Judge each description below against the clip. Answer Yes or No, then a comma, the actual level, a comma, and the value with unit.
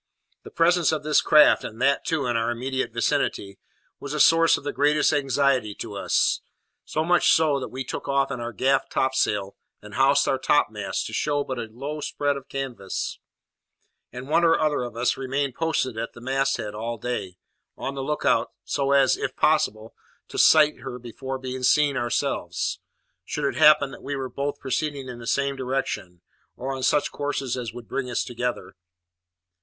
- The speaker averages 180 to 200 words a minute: Yes, average, 190 wpm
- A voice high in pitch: No, low, 135 Hz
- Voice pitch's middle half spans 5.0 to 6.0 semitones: No, average, 3.1 semitones